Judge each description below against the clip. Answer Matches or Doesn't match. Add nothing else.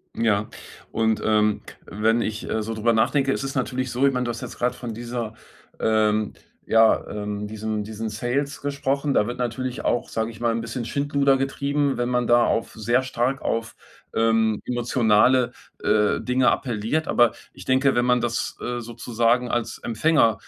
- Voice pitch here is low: Matches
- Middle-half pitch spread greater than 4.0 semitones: Doesn't match